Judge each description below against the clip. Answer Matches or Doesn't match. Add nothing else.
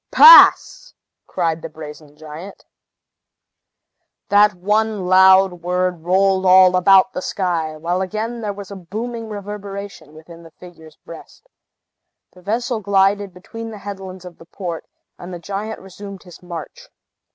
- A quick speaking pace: Doesn't match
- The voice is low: Doesn't match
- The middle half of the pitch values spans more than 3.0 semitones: Doesn't match